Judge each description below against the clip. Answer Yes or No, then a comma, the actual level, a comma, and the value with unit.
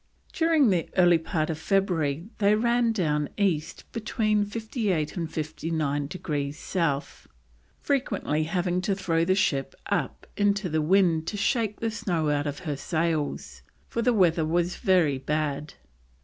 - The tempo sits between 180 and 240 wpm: No, average, 150 wpm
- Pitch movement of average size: Yes, average, 4.8 semitones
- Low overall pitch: No, medium, 175 Hz